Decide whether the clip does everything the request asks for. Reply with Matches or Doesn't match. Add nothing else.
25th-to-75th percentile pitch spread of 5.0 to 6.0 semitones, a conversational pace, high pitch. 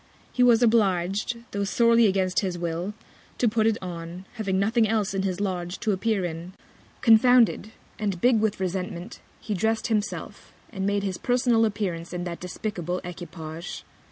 Doesn't match